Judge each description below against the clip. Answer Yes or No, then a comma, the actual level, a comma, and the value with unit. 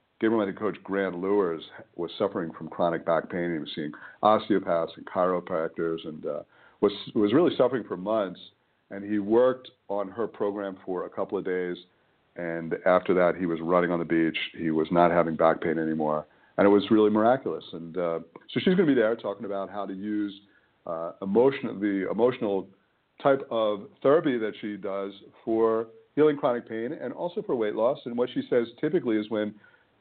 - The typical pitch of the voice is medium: No, low, 100 Hz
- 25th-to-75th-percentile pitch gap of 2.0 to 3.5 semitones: No, average, 3.9 semitones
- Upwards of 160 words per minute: Yes, average, 190 wpm